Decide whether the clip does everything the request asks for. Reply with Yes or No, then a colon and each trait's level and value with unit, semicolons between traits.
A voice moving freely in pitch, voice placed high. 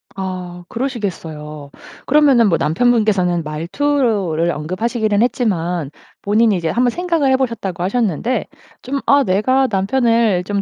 Yes: wide, 5.8 semitones; high, 210 Hz